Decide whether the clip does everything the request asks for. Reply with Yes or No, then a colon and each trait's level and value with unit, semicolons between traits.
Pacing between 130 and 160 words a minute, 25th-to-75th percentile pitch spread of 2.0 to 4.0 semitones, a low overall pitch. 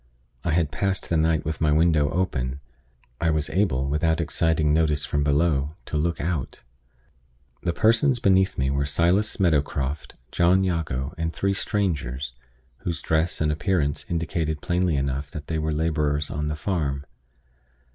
Yes: average, 155 wpm; average, 3.0 semitones; very low, 80 Hz